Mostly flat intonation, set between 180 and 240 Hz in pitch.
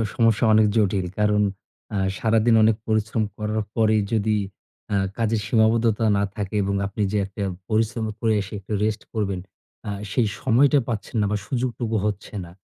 No: narrow, 1.5 semitones; low, 110 Hz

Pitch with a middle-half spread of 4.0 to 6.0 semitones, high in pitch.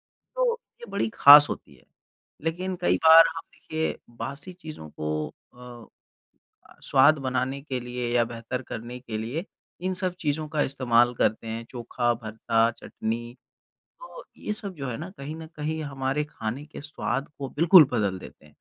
No: average, 5.0 semitones; low, 135 Hz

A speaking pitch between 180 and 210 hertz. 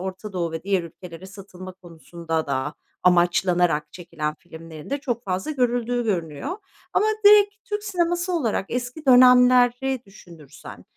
Yes: high, 190 Hz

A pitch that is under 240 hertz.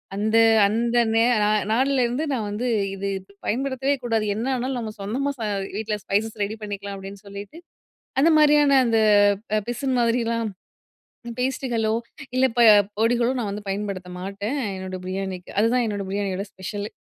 Yes: high, 225 Hz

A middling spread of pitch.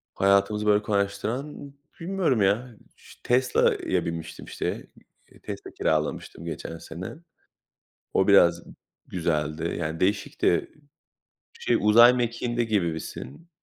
No: wide, 6.1 semitones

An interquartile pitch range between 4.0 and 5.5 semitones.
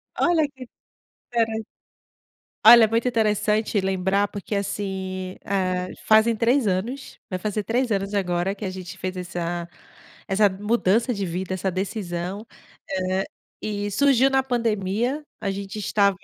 No: average, 3.2 semitones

